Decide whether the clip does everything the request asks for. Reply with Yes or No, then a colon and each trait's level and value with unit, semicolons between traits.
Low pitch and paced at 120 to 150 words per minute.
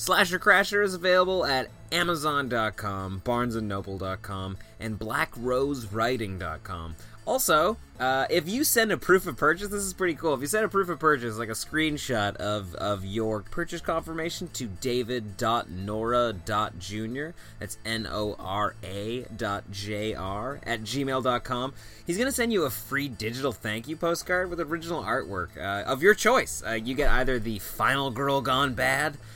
Yes: low, 125 Hz; average, 145 wpm